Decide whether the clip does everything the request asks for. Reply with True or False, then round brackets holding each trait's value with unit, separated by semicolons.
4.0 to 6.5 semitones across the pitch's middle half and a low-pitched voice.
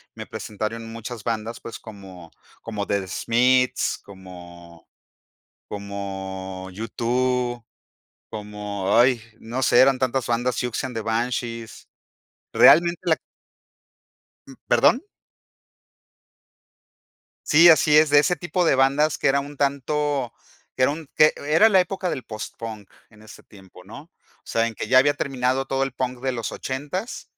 True (4.5 semitones; 120 Hz)